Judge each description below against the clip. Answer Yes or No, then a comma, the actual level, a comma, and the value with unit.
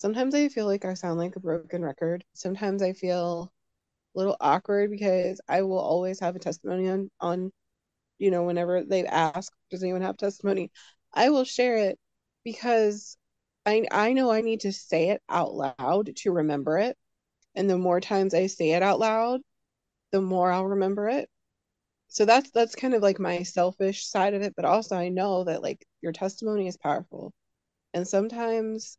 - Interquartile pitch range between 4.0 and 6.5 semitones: No, average, 2.8 semitones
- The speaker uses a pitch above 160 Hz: Yes, high, 190 Hz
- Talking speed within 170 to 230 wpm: Yes, average, 185 wpm